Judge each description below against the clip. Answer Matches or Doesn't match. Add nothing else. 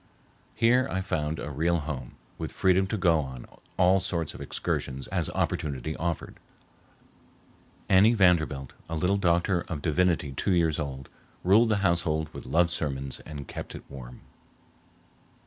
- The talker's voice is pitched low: Matches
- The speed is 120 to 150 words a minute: Matches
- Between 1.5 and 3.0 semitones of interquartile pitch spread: Doesn't match